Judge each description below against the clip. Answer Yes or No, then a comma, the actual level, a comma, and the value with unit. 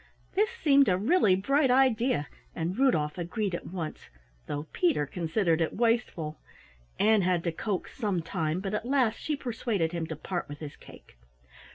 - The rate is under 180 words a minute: Yes, average, 170 wpm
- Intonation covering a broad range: Yes, wide, 7.1 semitones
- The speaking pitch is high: Yes, high, 195 Hz